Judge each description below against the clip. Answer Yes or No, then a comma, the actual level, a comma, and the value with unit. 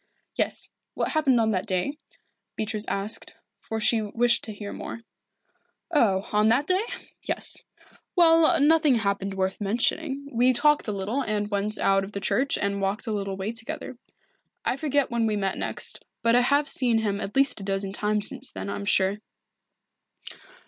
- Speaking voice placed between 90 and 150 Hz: No, high, 220 Hz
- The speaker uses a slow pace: No, average, 175 wpm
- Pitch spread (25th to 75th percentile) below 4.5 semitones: No, average, 5.1 semitones